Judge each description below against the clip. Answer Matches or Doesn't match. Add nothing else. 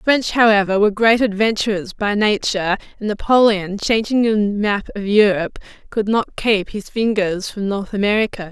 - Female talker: Matches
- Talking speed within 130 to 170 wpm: Matches